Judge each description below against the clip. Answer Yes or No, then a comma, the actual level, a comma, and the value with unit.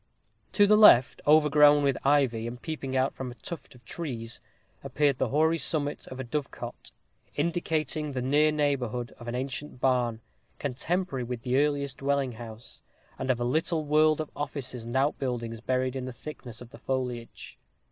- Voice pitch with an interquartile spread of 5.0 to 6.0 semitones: No, average, 3.3 semitones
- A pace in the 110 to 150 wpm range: No, average, 170 wpm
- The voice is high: No, low, 135 Hz